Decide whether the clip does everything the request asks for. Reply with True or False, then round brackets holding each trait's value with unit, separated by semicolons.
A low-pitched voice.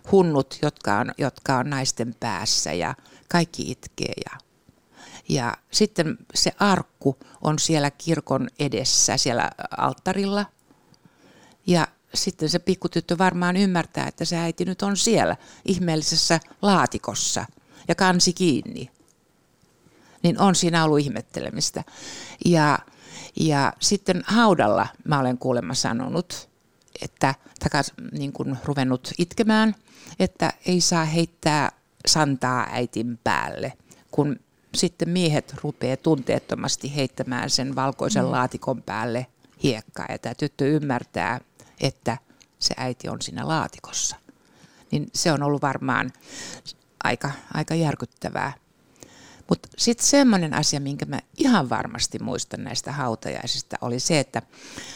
False (150 Hz)